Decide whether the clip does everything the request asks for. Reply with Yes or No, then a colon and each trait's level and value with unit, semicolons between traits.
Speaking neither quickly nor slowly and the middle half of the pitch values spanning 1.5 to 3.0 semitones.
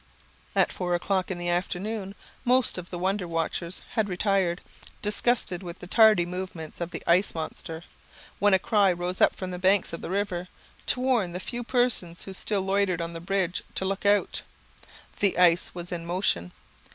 Yes: average, 180 wpm; narrow, 2.5 semitones